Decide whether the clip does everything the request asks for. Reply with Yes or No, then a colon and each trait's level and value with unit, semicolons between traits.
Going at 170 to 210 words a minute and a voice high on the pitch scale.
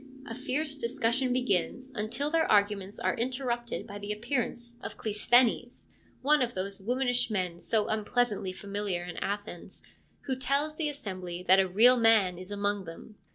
No: average, 155 wpm; high, 225 Hz